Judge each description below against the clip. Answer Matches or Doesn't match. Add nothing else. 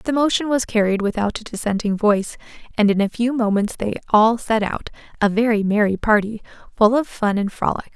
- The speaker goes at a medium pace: Matches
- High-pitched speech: Matches